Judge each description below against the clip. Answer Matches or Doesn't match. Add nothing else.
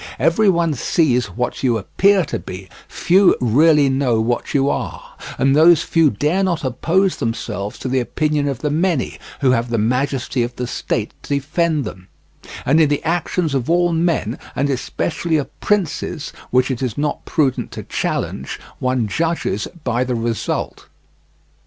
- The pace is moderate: Matches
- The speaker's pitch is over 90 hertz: Matches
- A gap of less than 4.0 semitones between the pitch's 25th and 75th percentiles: Doesn't match